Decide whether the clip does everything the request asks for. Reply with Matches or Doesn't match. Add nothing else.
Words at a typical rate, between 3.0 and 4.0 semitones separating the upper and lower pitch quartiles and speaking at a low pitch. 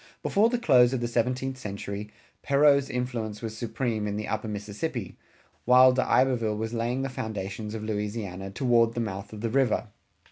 Matches